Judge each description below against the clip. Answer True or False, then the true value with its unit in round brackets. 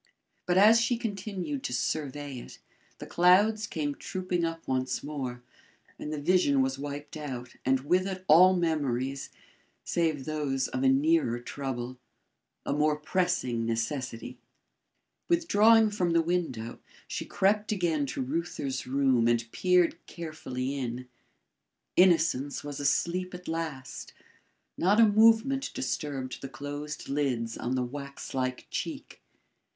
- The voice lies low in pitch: False (150 Hz)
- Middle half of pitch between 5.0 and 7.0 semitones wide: True (5.5 semitones)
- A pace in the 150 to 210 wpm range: False (135 wpm)